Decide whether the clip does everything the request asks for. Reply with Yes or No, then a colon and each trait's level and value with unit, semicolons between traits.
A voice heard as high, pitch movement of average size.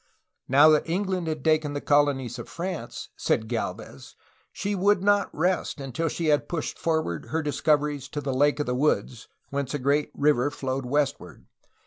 No: medium, 145 Hz; average, 3.1 semitones